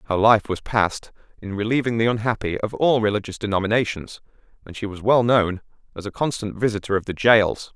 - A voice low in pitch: Yes, low, 105 Hz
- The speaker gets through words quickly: No, average, 185 wpm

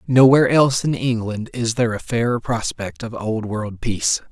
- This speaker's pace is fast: No, average, 180 wpm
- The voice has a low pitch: Yes, low, 115 Hz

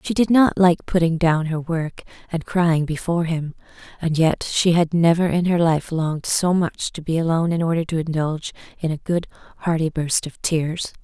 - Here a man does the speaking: No, female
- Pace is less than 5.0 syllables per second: No, 5.1 syllables/s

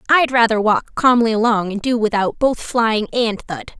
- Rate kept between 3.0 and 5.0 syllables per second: Yes, 4.6 syllables/s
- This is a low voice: No, high, 225 Hz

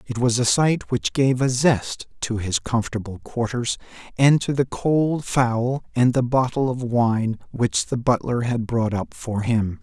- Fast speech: No, average, 185 wpm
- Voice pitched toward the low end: Yes, low, 120 Hz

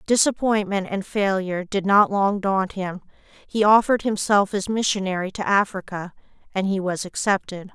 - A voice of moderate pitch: No, high, 195 Hz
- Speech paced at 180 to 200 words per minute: No, average, 140 wpm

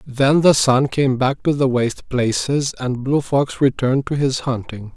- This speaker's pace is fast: No, average, 195 wpm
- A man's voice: Yes, male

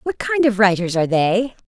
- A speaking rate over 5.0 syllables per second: Yes, 5.4 syllables/s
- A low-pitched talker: No, high, 215 Hz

